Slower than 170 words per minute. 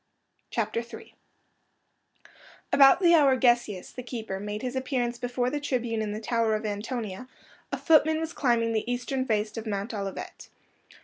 Yes: average, 160 wpm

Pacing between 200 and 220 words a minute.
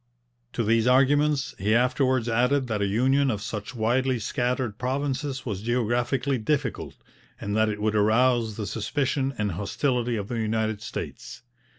No: average, 155 wpm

